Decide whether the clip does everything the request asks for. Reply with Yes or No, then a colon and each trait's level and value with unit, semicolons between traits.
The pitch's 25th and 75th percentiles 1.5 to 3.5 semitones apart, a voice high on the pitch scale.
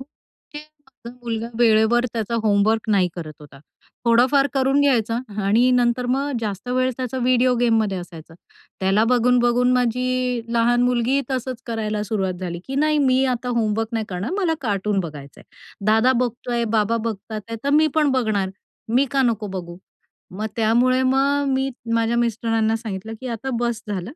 Yes: average, 2.9 semitones; high, 235 Hz